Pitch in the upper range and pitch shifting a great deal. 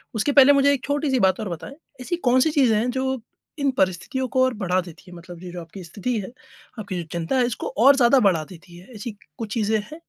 Yes: high, 225 Hz; wide, 6.3 semitones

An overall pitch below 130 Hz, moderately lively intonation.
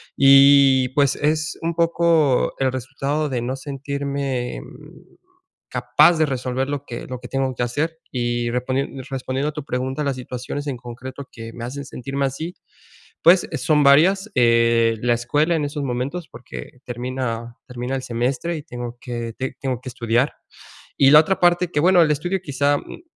No: low, 135 Hz; average, 3.1 semitones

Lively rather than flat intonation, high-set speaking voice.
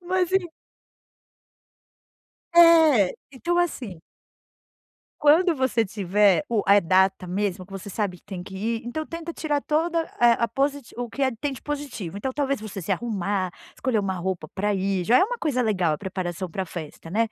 Yes: wide, 7.5 semitones; high, 225 Hz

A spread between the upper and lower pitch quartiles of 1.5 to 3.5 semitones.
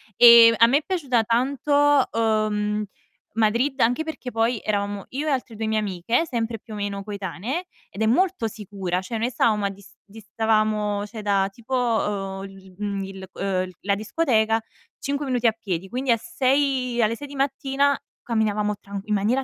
No: average, 3.9 semitones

